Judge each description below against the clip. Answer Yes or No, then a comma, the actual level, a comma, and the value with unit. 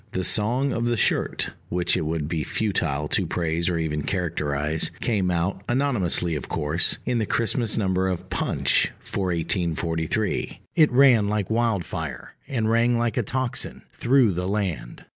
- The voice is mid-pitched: No, very low, 95 Hz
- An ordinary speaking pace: Yes, average, 160 wpm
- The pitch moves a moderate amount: No, wide, 6.0 semitones